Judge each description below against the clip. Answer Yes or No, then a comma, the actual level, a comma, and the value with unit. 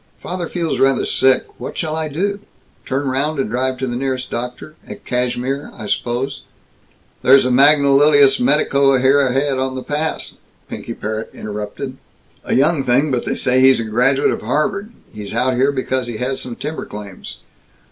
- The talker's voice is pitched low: Yes, low, 130 Hz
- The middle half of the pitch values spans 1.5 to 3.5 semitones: Yes, narrow, 2.4 semitones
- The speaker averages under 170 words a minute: No, average, 175 wpm